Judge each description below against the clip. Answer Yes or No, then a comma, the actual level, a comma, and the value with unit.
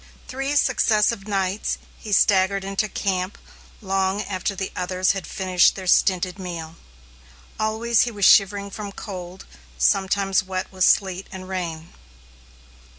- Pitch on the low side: No, high, 195 Hz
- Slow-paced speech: Yes, slow, 130 wpm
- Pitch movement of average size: No, narrow, 1.7 semitones